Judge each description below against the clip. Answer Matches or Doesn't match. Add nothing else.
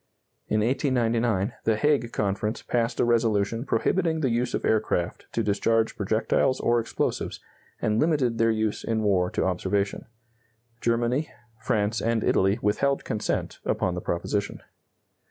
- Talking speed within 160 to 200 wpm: Doesn't match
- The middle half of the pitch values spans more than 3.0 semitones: Doesn't match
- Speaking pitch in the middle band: Doesn't match